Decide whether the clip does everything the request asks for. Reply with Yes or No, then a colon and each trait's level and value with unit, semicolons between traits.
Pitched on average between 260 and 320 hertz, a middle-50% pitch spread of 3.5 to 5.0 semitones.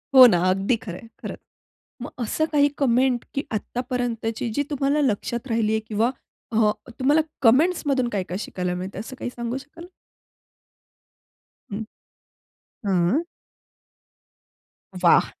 No: high, 235 Hz; average, 4.0 semitones